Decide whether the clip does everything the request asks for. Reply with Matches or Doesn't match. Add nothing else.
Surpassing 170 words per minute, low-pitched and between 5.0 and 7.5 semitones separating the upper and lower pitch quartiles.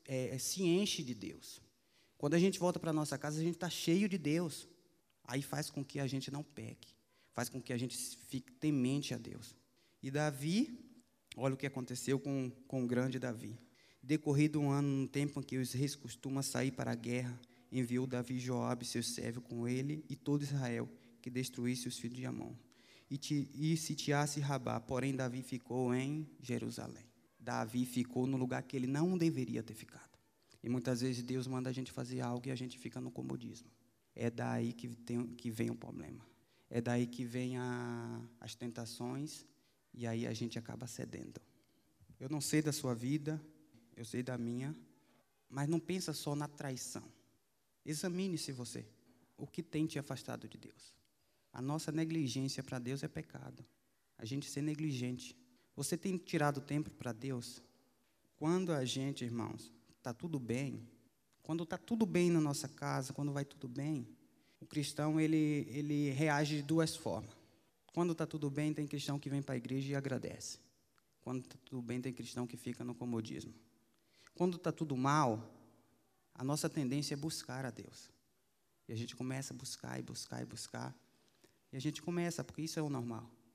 Doesn't match